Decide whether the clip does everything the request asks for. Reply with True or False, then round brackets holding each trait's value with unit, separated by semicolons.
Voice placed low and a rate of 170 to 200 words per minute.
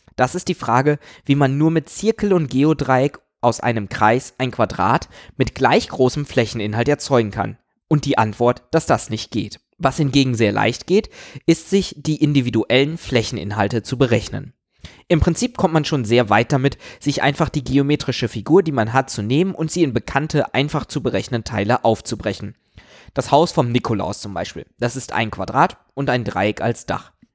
True (130 Hz; 180 wpm)